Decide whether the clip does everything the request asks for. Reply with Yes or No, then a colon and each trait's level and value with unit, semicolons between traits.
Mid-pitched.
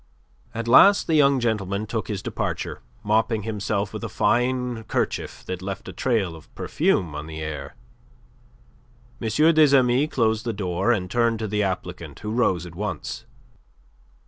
No: low, 110 Hz